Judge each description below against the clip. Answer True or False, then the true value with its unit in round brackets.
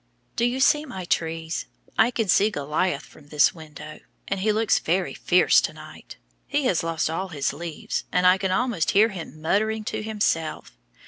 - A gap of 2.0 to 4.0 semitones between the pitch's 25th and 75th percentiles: False (5.1 semitones)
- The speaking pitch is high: False (180 Hz)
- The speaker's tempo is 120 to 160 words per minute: False (180 wpm)